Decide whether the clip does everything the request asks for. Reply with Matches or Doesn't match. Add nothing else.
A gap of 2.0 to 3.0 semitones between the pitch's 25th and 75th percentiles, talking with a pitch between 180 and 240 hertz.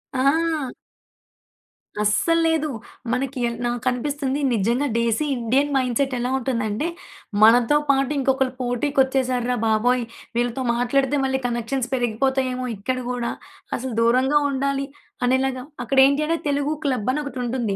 Doesn't match